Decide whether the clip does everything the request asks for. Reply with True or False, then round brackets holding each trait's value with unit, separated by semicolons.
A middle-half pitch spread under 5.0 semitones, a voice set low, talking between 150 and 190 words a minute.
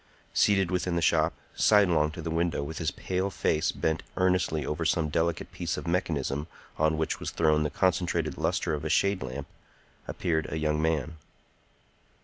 True (2.4 semitones; 80 Hz; 170 wpm)